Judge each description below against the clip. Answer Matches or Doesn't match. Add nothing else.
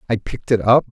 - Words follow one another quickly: Matches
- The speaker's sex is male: Matches